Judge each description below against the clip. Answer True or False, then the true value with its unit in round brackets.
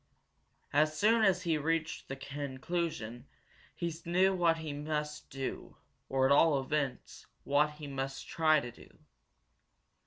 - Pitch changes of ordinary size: True (3.1 semitones)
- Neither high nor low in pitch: True (150 Hz)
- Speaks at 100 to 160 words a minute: True (135 wpm)